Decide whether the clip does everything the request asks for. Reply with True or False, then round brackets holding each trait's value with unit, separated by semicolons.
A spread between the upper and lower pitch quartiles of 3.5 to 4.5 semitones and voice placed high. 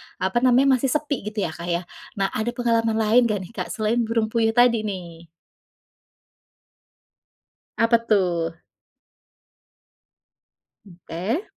True (4.1 semitones; 220 Hz)